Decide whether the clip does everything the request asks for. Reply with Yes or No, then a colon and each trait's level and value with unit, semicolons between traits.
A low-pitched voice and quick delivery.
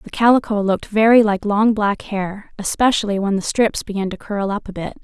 No: high, 205 Hz; fast, 215 wpm